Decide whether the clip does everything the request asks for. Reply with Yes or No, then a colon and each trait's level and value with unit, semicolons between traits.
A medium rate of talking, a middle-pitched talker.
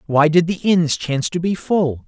No: fast, 230 wpm; medium, 165 Hz